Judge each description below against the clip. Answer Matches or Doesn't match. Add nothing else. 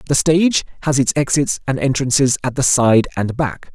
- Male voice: Matches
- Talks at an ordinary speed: Matches